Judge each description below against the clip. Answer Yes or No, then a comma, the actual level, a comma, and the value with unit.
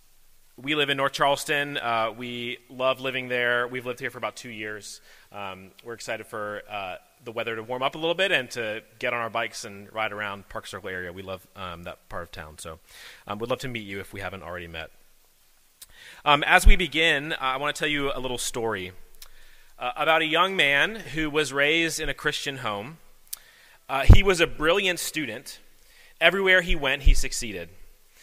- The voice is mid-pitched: No, low, 125 Hz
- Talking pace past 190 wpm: Yes, fast, 205 wpm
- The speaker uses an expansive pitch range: Yes, wide, 5.9 semitones